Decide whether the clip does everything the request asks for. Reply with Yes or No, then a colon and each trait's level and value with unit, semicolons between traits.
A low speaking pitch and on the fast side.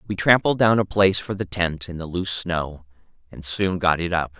Yes: very low, 90 Hz; fast, 230 wpm